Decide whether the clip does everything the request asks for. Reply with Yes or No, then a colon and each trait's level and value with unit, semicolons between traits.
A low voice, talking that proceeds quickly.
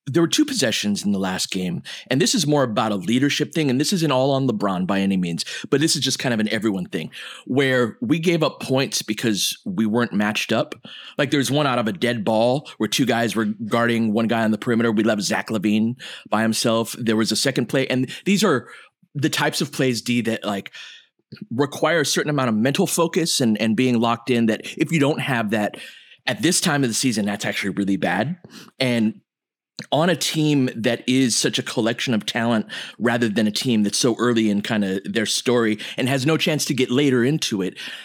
Yes: low, 120 Hz; fast, 225 wpm